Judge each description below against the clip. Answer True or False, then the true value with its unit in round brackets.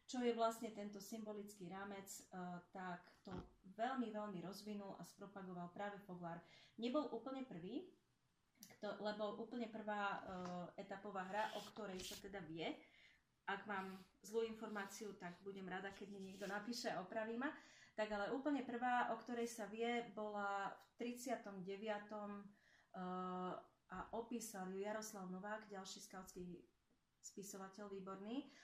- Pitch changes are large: False (2.9 semitones)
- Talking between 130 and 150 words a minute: True (140 wpm)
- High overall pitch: True (205 Hz)